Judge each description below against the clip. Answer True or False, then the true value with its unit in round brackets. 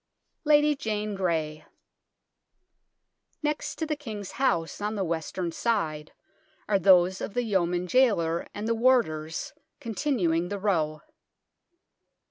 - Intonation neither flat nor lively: False (5.7 semitones)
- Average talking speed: False (115 wpm)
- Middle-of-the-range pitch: False (200 Hz)